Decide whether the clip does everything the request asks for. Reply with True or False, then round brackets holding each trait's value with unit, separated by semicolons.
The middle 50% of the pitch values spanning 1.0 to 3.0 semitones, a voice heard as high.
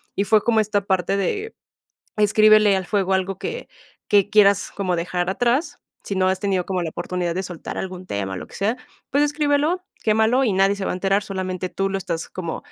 True (2.7 semitones; 195 Hz)